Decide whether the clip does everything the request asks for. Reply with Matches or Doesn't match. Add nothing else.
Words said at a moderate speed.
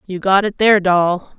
Doesn't match